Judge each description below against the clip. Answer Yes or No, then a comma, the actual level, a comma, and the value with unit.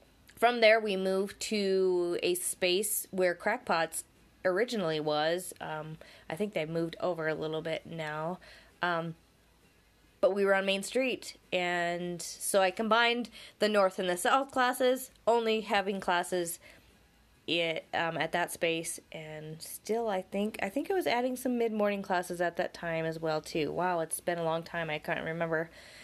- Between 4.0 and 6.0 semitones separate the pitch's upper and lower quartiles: Yes, average, 4.5 semitones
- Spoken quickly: No, average, 170 wpm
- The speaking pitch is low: No, medium, 180 Hz